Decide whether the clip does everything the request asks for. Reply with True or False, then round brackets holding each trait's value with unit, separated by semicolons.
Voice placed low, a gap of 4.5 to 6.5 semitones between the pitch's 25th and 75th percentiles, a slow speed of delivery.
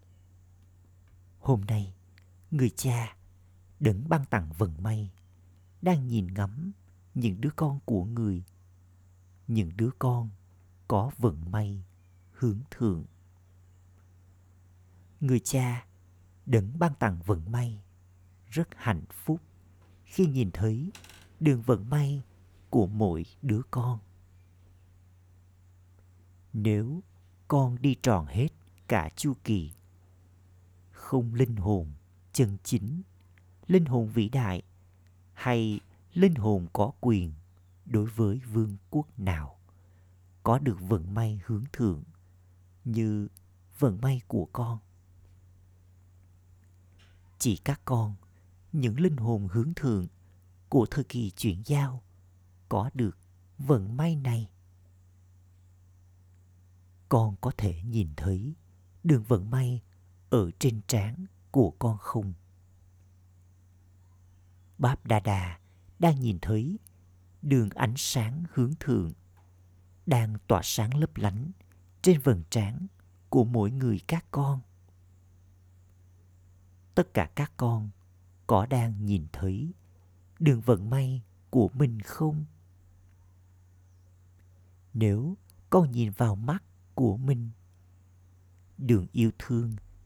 True (95 Hz; 4.8 semitones; 110 wpm)